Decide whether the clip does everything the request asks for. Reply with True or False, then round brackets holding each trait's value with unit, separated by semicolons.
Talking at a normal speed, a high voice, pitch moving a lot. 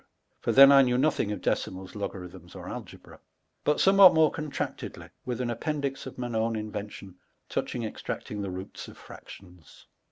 False (160 wpm; 115 Hz; 5.8 semitones)